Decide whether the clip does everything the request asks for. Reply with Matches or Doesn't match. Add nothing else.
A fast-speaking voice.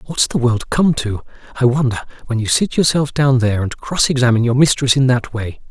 Matches